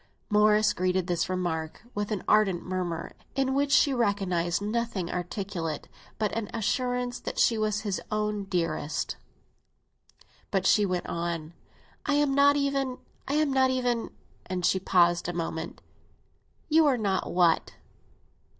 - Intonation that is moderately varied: No, wide, 5.8 semitones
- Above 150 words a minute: No, average, 140 wpm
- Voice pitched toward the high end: Yes, high, 205 Hz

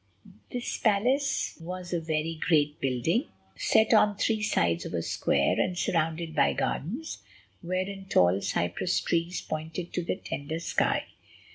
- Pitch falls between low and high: Yes, medium, 170 Hz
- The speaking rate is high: No, average, 140 wpm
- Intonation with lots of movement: No, average, 4.3 semitones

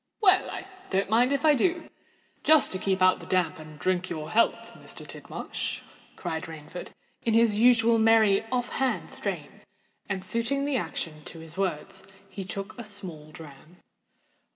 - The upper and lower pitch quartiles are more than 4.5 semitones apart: Yes, wide, 5.4 semitones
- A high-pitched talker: Yes, high, 195 Hz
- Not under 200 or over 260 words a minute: No, average, 155 wpm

